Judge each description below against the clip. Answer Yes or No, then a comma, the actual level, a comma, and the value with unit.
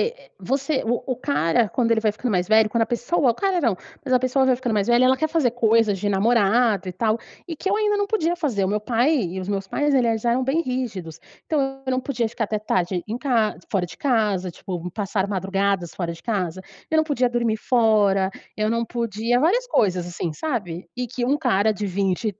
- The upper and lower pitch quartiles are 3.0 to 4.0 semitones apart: No, average, 4.6 semitones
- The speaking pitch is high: Yes, high, 230 Hz